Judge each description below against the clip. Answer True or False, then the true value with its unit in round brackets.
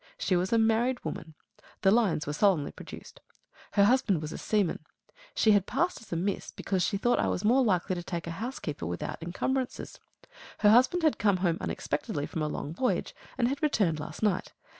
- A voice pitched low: False (200 Hz)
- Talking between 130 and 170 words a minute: False (200 wpm)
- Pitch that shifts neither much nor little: False (6.1 semitones)